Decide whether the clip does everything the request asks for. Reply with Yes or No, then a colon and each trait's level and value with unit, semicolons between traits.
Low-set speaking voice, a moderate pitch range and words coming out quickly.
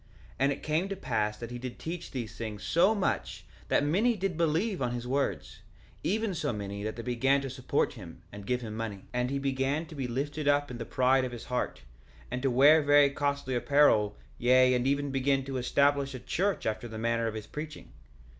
Yes: low, 130 Hz; average, 3.5 semitones; fast, 220 wpm